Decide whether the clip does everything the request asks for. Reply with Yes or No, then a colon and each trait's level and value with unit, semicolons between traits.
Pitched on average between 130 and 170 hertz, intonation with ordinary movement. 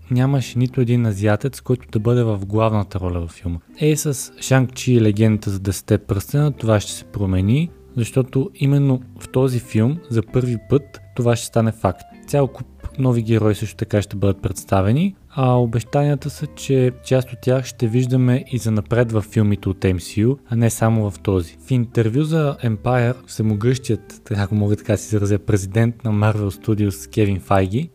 No: low, 115 Hz; average, 3.6 semitones